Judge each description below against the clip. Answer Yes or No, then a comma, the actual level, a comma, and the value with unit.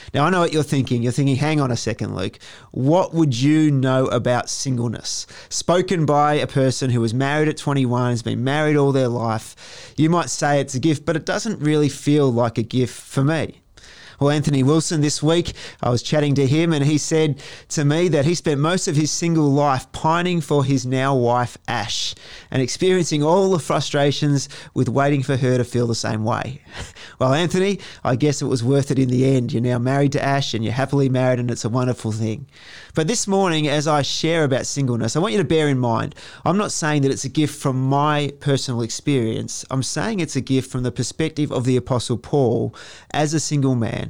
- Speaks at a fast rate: Yes, fast, 220 wpm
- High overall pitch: No, medium, 140 Hz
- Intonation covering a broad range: No, average, 3.5 semitones